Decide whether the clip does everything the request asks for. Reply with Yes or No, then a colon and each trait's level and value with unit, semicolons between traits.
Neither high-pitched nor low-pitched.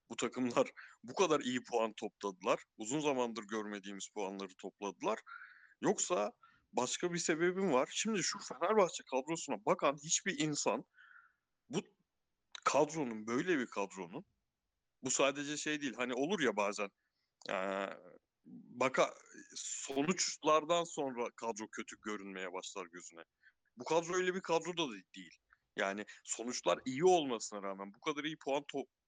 No: low, 130 Hz